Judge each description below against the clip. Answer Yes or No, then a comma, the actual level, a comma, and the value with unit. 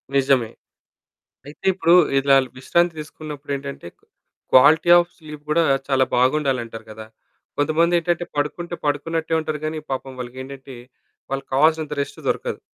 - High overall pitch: No, medium, 145 Hz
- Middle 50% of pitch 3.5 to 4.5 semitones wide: No, average, 3.1 semitones